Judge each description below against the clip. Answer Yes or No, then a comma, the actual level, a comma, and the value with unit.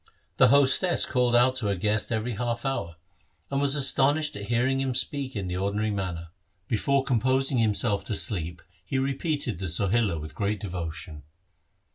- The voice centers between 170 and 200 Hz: No, low, 115 Hz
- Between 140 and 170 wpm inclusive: Yes, average, 165 wpm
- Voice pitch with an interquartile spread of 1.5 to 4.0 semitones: No, average, 5.2 semitones